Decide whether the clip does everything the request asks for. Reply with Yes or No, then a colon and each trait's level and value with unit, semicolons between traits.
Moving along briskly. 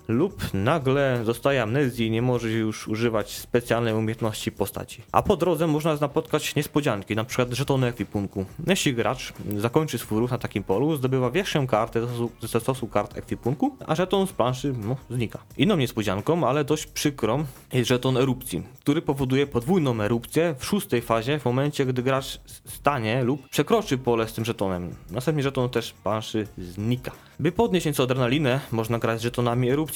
Yes: fast, 170 wpm